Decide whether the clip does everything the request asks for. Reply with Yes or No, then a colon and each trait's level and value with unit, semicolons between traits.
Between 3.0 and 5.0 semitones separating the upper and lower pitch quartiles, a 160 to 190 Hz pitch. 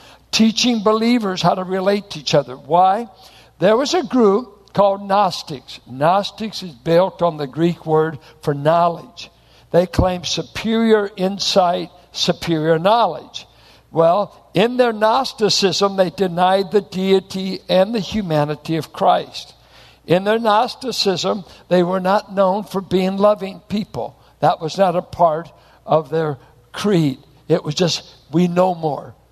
Yes: average, 4.0 semitones; medium, 185 Hz